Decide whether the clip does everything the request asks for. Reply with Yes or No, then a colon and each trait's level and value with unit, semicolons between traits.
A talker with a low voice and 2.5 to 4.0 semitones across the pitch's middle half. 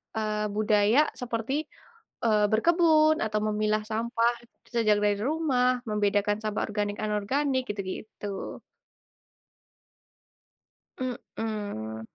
No: high, 215 Hz; average, 3.2 semitones